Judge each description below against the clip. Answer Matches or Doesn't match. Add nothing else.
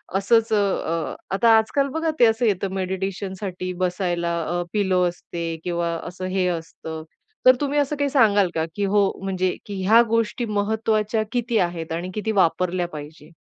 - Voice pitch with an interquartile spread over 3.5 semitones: Matches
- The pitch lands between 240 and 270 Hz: Doesn't match